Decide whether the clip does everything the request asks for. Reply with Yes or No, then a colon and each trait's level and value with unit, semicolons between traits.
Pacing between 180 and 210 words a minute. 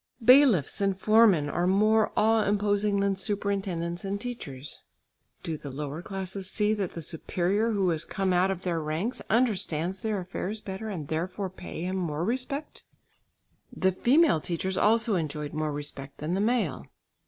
No: average, 160 wpm